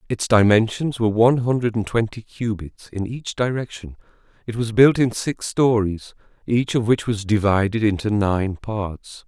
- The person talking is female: No, male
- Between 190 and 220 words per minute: No, average, 160 wpm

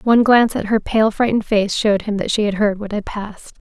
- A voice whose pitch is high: Yes, high, 210 Hz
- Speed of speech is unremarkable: No, fast, 260 wpm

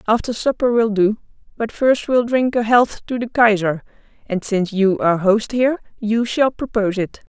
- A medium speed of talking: Yes, average, 190 wpm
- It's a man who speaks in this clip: No, female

